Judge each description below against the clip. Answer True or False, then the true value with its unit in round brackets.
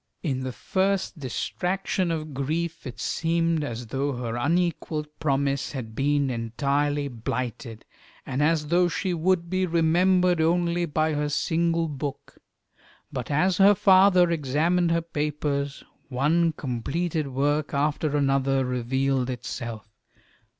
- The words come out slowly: True (125 wpm)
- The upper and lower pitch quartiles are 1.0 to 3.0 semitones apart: False (4.0 semitones)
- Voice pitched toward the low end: False (150 Hz)